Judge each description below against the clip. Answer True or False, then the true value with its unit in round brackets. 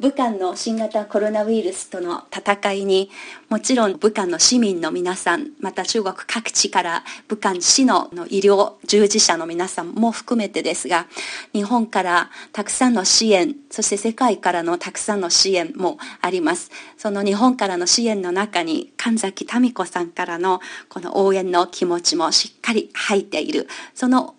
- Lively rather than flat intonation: False (4.6 semitones)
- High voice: True (205 Hz)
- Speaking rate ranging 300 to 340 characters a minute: True (320 characters per minute)